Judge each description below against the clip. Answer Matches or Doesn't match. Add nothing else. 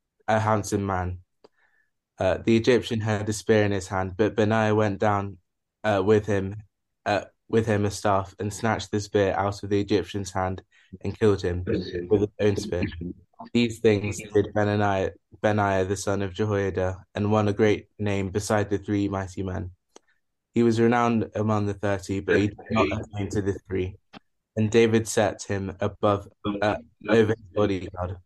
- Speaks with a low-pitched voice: Matches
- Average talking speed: Matches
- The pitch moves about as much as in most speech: Doesn't match